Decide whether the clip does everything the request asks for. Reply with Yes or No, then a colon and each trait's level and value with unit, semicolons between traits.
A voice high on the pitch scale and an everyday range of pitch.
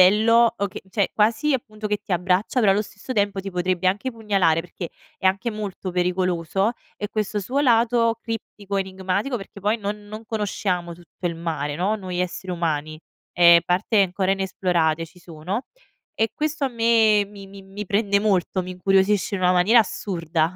Yes: high, 195 Hz; average, 3.0 semitones